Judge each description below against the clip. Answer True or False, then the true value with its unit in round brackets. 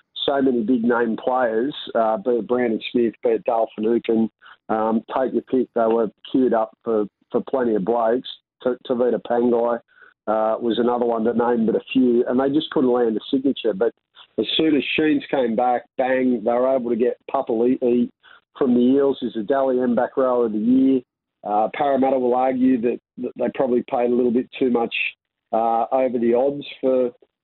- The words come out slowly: False (195 wpm)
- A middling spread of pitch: False (1.9 semitones)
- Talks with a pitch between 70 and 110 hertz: False (120 Hz)